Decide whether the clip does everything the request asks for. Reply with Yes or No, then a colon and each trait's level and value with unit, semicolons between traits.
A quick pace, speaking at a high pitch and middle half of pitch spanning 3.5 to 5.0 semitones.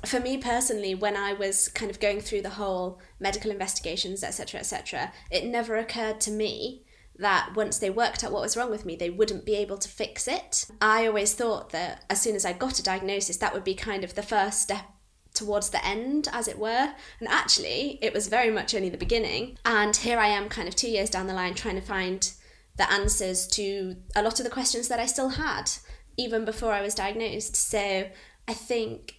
No: fast, 220 wpm; high, 210 Hz; narrow, 2.5 semitones